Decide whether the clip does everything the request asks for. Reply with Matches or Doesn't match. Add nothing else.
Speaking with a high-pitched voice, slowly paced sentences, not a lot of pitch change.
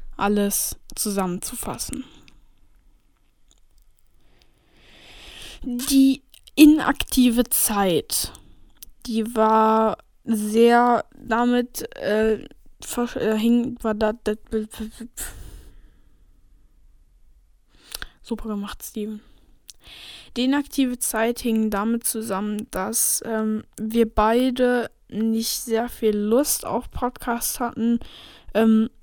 Matches